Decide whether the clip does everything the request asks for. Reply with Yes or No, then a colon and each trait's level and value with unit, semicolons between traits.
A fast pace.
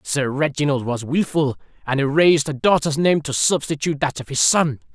No: average, 180 wpm